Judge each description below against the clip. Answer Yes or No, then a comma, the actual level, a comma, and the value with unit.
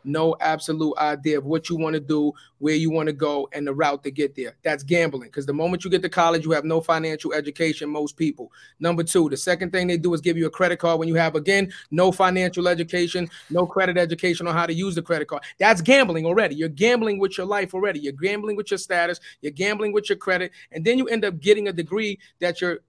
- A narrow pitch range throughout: No, average, 3.0 semitones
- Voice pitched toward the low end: No, medium, 170 Hz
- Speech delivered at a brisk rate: Yes, fast, 250 wpm